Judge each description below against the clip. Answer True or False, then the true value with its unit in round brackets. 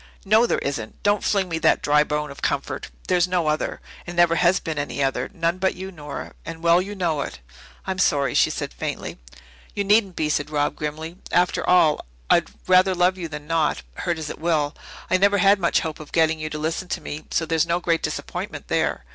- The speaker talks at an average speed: False (220 wpm)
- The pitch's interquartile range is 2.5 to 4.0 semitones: True (3.2 semitones)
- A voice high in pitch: False (165 Hz)